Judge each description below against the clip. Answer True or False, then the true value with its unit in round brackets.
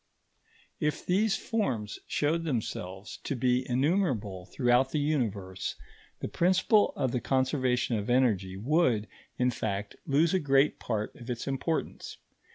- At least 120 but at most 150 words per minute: True (135 wpm)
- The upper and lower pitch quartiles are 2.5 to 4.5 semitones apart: False (5.6 semitones)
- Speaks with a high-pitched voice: False (130 Hz)